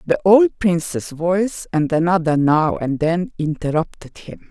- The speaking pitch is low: No, medium, 170 Hz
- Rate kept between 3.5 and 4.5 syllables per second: Yes, 4.3 syllables/s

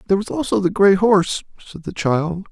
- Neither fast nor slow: No, fast, 215 wpm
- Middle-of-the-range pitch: Yes, medium, 180 Hz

